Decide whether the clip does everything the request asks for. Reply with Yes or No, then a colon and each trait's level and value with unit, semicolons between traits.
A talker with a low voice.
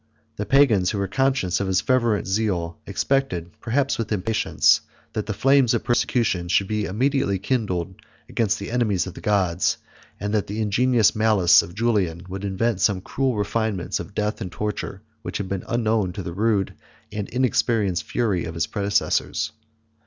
Yes: low, 105 Hz